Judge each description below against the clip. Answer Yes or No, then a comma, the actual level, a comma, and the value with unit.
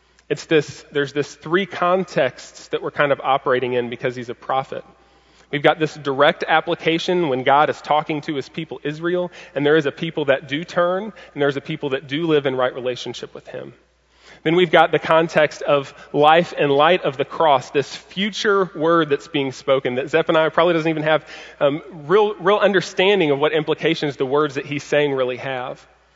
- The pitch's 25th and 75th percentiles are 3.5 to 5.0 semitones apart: No, average, 3.0 semitones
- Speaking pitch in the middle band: Yes, medium, 155 Hz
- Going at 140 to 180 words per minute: No, average, 200 wpm